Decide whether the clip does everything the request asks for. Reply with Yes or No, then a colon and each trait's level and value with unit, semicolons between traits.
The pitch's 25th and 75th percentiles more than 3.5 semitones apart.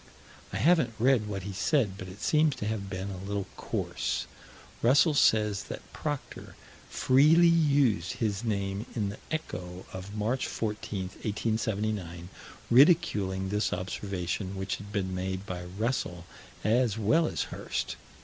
Yes: average, 4.5 semitones